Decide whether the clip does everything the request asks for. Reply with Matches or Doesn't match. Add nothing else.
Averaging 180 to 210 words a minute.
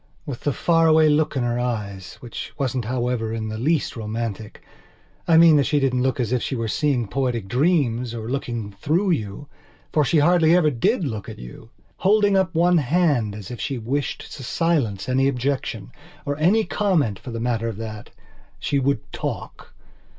Doesn't match